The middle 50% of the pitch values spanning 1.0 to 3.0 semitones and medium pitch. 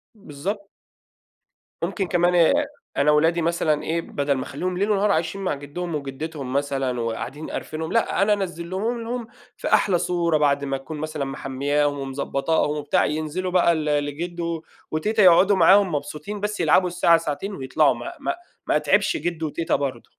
No: average, 4.3 semitones; medium, 160 Hz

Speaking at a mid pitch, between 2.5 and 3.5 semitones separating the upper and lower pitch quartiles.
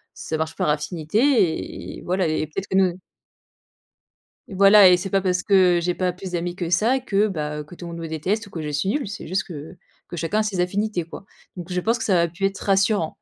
Yes: medium, 180 Hz; average, 2.9 semitones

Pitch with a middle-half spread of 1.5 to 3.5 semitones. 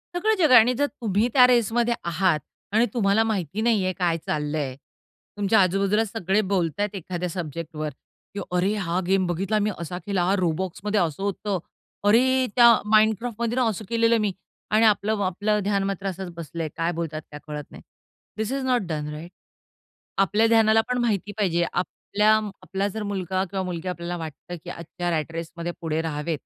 No: average, 4.1 semitones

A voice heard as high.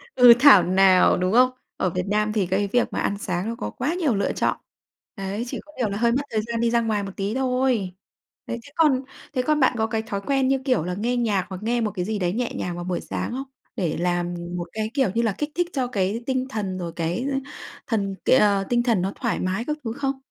Yes: high, 220 Hz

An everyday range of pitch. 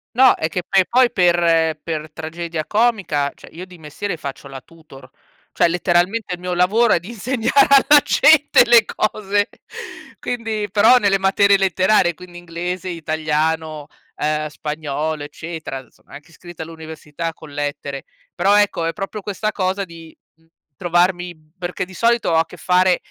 Yes: average, 4.2 semitones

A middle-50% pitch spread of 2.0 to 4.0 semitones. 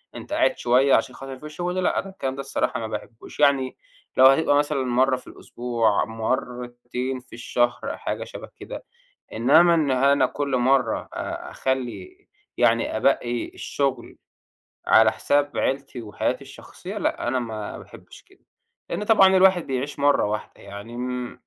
Yes: average, 2.9 semitones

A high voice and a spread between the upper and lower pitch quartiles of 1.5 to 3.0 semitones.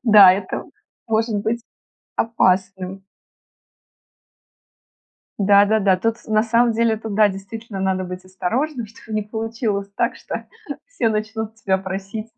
Yes: high, 215 Hz; average, 2.7 semitones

